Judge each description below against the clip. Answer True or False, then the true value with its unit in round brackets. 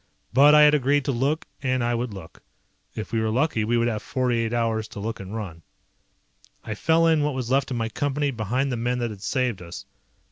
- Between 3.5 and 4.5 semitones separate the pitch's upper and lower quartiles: True (3.8 semitones)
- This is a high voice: False (120 Hz)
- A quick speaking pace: True (235 wpm)